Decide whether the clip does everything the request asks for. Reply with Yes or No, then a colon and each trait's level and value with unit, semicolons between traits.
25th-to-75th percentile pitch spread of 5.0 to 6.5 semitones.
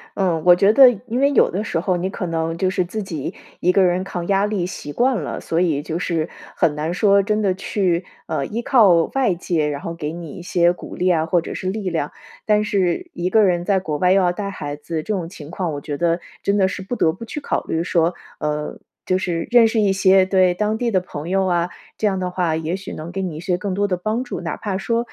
No: average, 3.1 semitones